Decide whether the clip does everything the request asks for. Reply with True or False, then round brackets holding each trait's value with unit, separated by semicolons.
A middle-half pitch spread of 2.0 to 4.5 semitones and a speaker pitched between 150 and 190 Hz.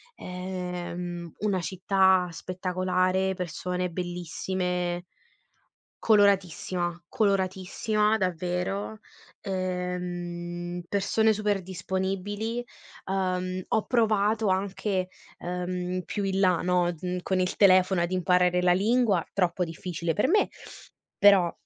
False (1.6 semitones; 185 Hz)